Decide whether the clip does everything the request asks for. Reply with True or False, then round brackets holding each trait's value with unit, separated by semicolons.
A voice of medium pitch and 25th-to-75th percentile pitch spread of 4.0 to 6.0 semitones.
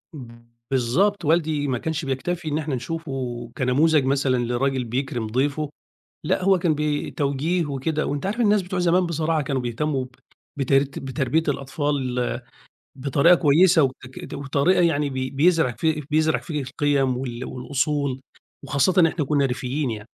False (145 Hz; 3.4 semitones)